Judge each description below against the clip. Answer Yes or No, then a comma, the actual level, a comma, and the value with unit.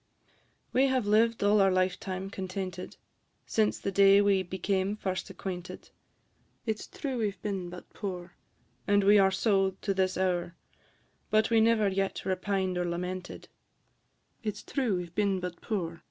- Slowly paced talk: No, average, 170 wpm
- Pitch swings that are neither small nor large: No, narrow, 2.2 semitones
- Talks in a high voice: Yes, high, 195 Hz